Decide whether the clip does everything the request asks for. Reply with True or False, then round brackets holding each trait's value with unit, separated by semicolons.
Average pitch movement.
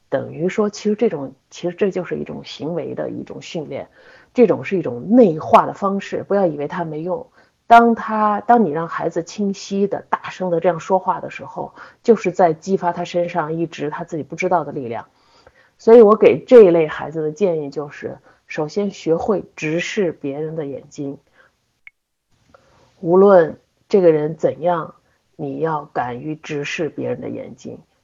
True (4.4 semitones)